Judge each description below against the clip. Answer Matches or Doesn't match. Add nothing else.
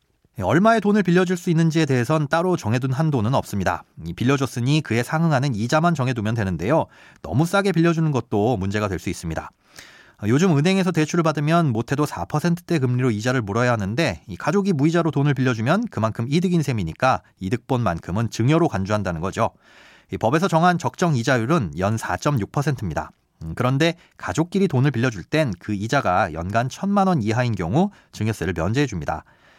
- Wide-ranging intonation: Matches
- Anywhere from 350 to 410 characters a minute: Matches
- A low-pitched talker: Matches